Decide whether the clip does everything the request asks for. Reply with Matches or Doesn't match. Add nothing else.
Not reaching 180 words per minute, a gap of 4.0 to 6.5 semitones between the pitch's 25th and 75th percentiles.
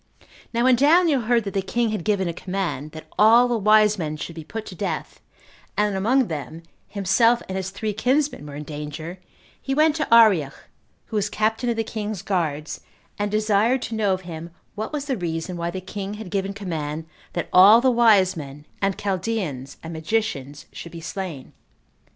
Doesn't match